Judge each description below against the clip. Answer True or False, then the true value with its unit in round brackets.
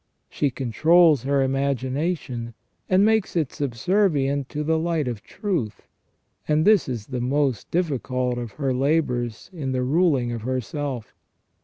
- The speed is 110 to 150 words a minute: True (140 wpm)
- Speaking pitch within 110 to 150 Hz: True (140 Hz)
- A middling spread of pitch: True (4.4 semitones)